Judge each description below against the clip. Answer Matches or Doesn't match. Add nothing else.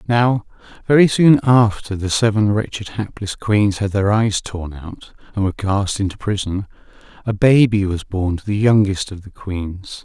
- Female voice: Doesn't match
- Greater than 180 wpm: Doesn't match